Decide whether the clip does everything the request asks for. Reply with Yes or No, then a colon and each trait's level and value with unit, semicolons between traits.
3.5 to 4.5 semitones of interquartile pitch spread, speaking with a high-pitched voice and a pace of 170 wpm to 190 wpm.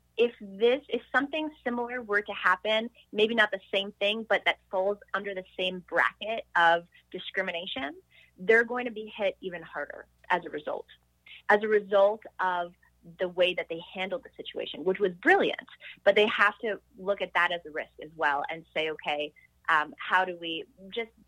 Yes: average, 4.1 semitones; high, 200 Hz; average, 185 wpm